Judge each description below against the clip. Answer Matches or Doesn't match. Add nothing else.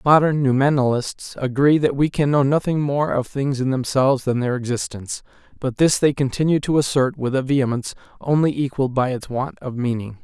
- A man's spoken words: Matches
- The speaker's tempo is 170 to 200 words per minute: Matches